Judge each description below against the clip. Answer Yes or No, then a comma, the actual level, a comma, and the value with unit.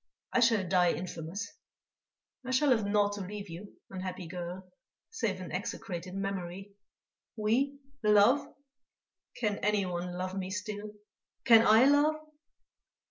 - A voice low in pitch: No, high, 205 Hz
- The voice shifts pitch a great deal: No, average, 3.3 semitones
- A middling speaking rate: No, slow, 125 wpm